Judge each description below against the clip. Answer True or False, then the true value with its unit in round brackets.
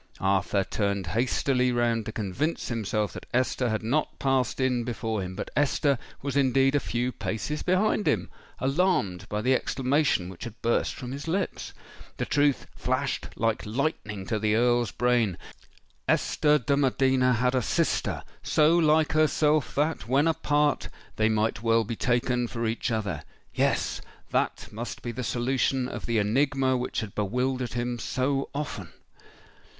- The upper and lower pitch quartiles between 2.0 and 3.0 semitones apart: False (4.0 semitones)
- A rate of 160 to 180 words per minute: False (145 wpm)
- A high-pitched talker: False (125 Hz)